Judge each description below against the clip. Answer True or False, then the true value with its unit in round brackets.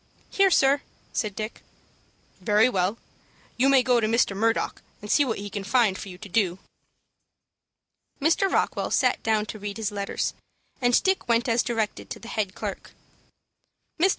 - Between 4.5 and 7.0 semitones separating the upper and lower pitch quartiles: False (3.4 semitones)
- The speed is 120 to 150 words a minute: False (170 wpm)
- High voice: True (225 Hz)